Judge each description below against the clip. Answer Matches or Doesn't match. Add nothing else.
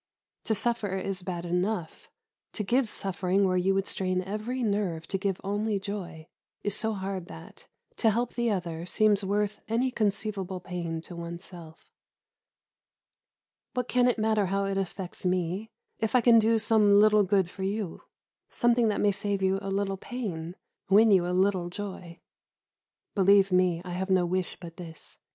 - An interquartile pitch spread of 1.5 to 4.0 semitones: Matches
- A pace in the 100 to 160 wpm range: Doesn't match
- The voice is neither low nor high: Doesn't match